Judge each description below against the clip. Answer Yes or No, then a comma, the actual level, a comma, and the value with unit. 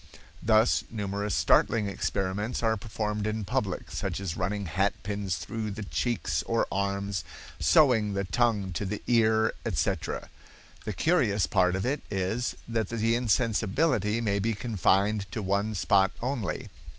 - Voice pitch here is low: Yes, low, 105 Hz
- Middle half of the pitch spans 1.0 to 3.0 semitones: Yes, narrow, 2.4 semitones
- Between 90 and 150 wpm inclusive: Yes, average, 140 wpm